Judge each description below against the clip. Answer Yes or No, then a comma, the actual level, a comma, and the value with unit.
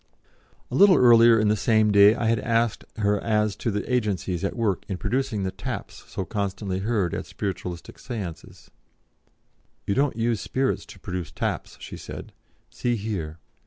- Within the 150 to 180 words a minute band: Yes, average, 165 wpm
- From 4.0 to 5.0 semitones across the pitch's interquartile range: No, average, 3.0 semitones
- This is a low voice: Yes, low, 105 Hz